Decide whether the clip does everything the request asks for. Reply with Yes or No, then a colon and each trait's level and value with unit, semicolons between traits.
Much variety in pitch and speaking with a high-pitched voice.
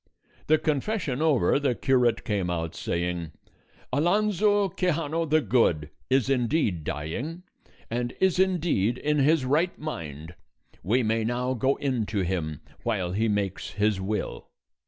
No: wide, 8.1 semitones; low, 125 Hz